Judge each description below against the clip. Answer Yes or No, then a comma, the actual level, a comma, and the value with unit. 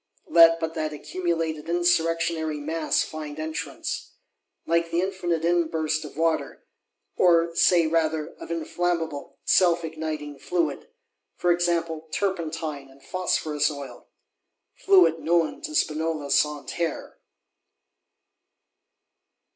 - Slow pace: Yes, slow, 100 wpm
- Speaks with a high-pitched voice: No, medium, 165 Hz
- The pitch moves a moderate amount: No, narrow, 1.7 semitones